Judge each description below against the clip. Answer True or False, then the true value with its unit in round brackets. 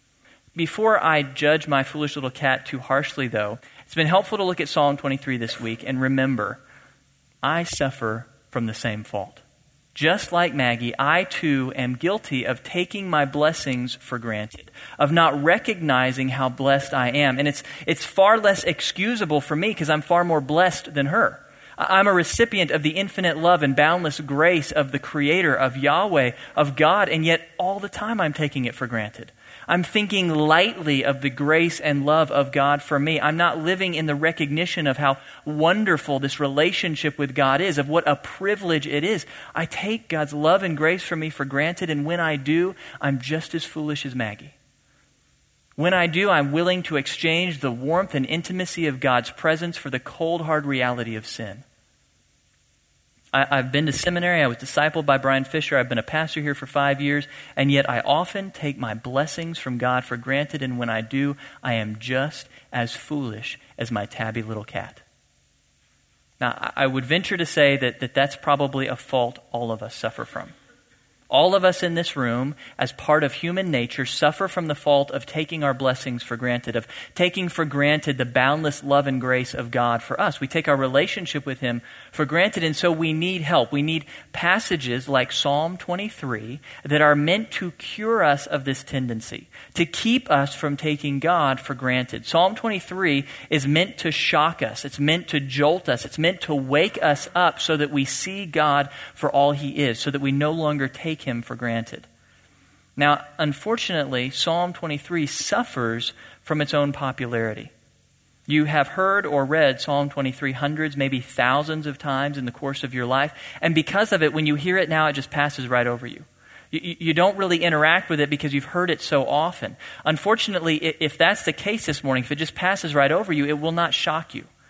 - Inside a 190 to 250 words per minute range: True (195 wpm)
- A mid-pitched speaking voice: True (145 Hz)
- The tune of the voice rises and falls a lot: False (3.6 semitones)